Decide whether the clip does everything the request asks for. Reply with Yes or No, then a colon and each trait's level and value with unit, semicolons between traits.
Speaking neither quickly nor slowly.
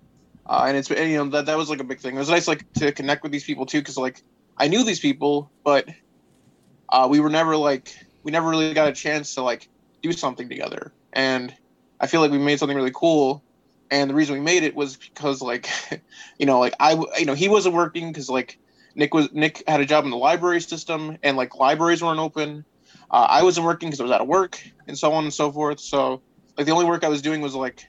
No: fast, 250 wpm